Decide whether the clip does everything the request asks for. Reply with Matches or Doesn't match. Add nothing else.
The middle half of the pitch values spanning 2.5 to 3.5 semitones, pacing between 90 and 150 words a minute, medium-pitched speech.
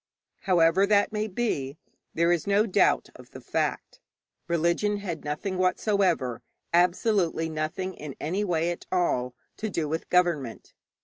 Doesn't match